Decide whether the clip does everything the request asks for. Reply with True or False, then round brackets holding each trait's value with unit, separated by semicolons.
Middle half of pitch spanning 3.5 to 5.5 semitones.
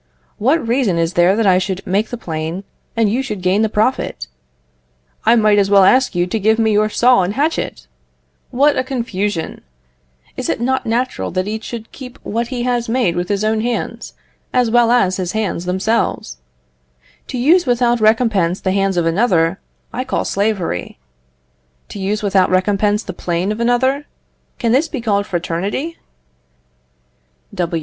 True (4.4 semitones)